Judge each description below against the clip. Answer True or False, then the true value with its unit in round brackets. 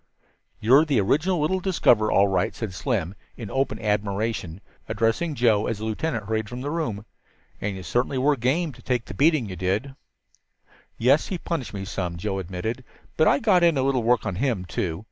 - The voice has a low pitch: True (115 Hz)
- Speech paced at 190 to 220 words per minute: True (195 wpm)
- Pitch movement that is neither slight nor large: False (5.9 semitones)